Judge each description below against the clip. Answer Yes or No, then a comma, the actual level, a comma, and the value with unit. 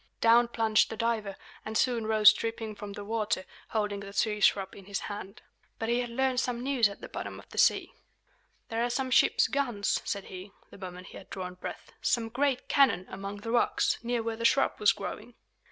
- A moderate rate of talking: No, fast, 210 wpm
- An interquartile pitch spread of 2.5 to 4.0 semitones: Yes, average, 2.9 semitones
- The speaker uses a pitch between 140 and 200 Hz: No, high, 220 Hz